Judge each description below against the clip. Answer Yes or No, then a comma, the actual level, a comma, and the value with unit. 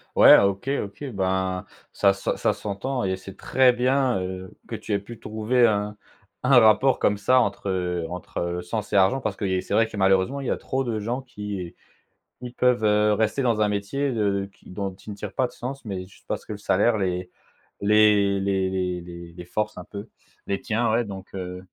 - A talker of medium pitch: No, low, 100 Hz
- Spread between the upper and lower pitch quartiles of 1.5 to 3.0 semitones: No, average, 3.5 semitones